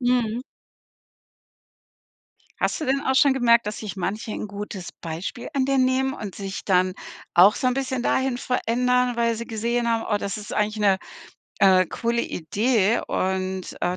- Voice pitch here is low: No, high, 230 Hz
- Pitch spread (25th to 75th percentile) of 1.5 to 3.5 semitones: No, average, 4.2 semitones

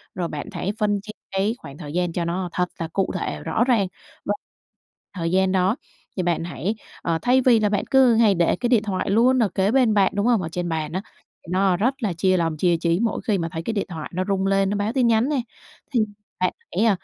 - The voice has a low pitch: No, high, 195 Hz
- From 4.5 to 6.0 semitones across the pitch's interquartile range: No, average, 4.1 semitones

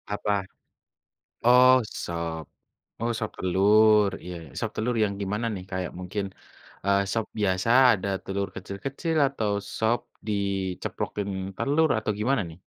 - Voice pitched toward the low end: Yes, low, 105 Hz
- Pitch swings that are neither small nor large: Yes, average, 3.3 semitones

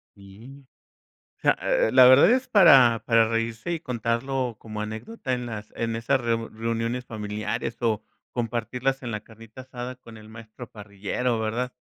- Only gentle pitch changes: Yes, narrow, 2.3 semitones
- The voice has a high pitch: No, low, 115 Hz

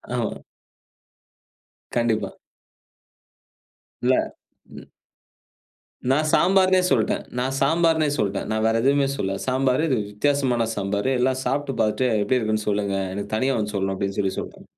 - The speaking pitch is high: No, low, 120 Hz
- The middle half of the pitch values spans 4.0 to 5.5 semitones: Yes, average, 4.9 semitones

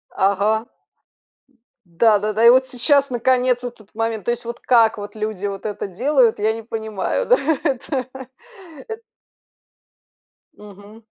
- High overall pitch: Yes, high, 225 Hz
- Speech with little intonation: No, average, 3.1 semitones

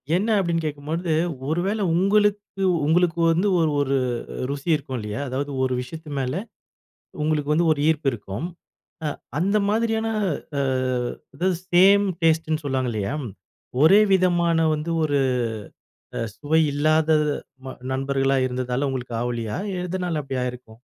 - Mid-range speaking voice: Yes, medium, 155 Hz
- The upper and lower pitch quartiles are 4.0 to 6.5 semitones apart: Yes, average, 4.6 semitones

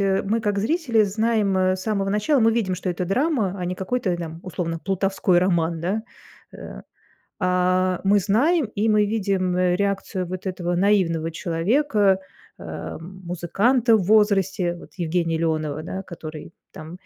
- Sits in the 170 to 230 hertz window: Yes, high, 190 Hz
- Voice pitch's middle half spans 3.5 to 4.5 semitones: No, average, 3.1 semitones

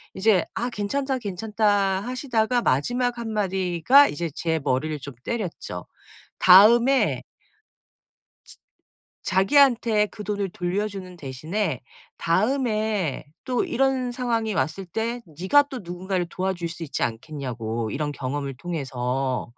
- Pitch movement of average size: No, wide, 6.7 semitones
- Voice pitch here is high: Yes, high, 195 Hz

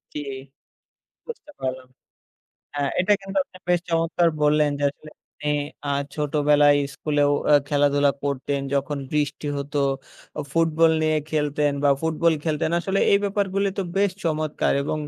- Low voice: No, medium, 150 Hz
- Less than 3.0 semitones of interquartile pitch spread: Yes, narrow, 2.4 semitones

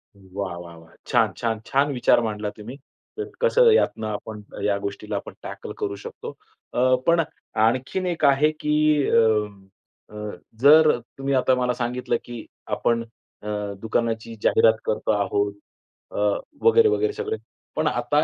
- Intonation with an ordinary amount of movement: No, wide, 5.9 semitones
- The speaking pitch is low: Yes, low, 120 Hz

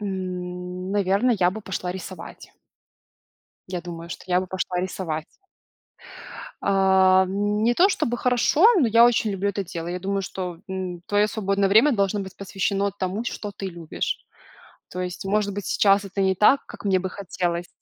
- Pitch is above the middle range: Yes, high, 195 Hz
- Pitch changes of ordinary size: No, narrow, 2.0 semitones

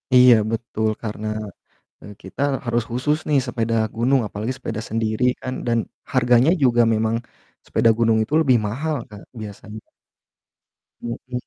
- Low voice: Yes, low, 115 Hz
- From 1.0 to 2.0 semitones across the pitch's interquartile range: No, narrow, 2.5 semitones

